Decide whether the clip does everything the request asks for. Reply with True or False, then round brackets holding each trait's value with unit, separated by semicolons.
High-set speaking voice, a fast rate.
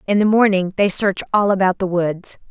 True (195 Hz; 215 wpm)